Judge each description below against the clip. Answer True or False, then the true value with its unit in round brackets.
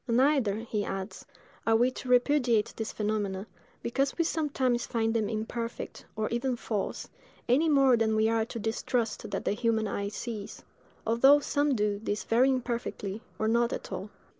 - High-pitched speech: True (230 Hz)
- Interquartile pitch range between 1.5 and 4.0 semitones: True (2.8 semitones)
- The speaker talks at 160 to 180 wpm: True (165 wpm)